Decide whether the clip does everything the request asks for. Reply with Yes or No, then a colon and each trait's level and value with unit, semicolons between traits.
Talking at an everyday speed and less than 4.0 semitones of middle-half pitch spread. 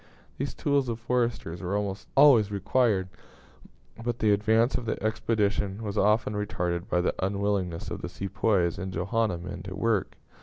Yes: average, 160 wpm; average, 3.0 semitones